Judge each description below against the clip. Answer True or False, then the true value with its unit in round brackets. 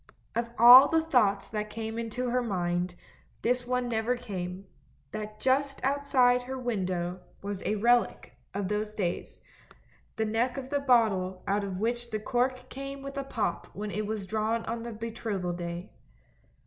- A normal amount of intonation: True (3.6 semitones)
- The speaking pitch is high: True (225 Hz)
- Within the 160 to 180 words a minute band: True (165 wpm)